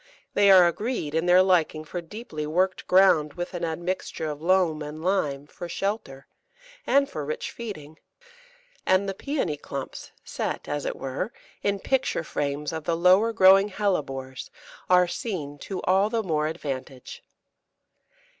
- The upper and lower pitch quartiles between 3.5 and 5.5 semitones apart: Yes, average, 4.4 semitones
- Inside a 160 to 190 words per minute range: No, average, 150 wpm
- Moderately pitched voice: Yes, medium, 175 Hz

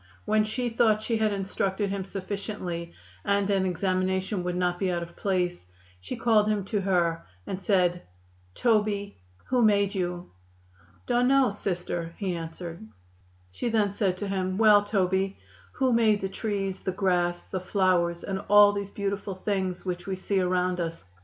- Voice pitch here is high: Yes, high, 195 Hz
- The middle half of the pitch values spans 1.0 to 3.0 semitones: Yes, narrow, 2.4 semitones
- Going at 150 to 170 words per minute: Yes, average, 165 wpm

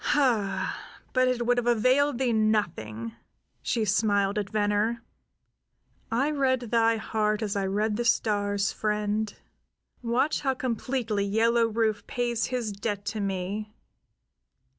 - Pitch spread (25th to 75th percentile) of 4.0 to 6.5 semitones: No, average, 2.7 semitones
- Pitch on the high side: Yes, high, 220 Hz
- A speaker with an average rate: No, slow, 130 wpm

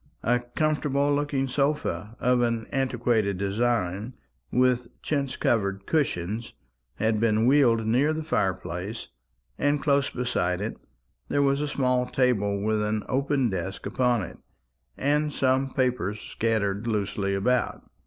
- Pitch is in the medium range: No, low, 120 Hz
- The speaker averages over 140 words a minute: No, slow, 135 wpm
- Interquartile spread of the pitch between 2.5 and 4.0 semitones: No, average, 4.5 semitones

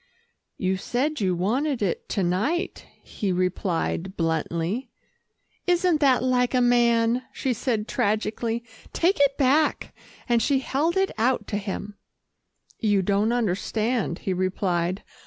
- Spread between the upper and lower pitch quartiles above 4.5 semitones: Yes, wide, 5.5 semitones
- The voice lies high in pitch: Yes, high, 225 Hz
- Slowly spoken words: Yes, slow, 130 wpm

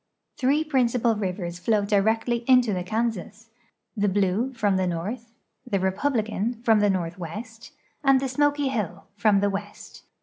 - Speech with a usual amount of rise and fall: Yes, average, 4.0 semitones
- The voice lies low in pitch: No, high, 215 Hz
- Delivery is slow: No, average, 145 wpm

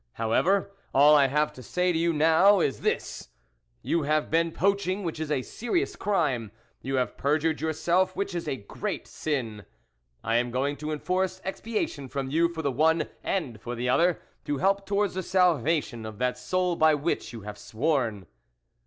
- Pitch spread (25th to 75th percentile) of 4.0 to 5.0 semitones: No, wide, 5.6 semitones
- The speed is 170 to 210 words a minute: Yes, average, 185 wpm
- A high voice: No, medium, 155 Hz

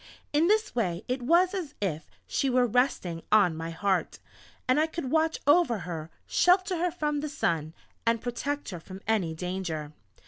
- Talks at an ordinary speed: Yes, average, 175 wpm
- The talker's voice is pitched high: Yes, high, 240 Hz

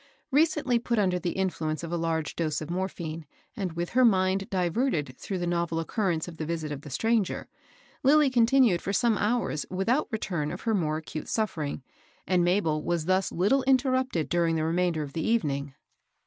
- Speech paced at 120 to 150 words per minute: No, average, 185 wpm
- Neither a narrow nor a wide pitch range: No, wide, 5.7 semitones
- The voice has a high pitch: No, medium, 180 Hz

